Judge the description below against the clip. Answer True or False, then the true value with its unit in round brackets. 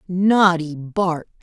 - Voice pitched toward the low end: False (175 Hz)